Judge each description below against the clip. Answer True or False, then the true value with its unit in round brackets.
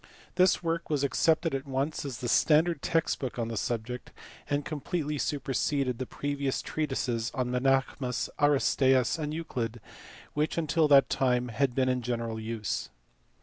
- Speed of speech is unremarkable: True (155 wpm)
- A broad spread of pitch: False (3.3 semitones)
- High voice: False (135 Hz)